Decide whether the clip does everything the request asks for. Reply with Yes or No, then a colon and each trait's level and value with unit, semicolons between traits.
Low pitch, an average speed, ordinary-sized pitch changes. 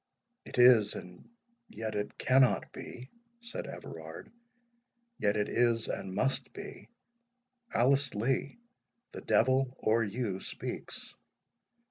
No: low, 120 Hz; slow, 105 wpm; average, 3.8 semitones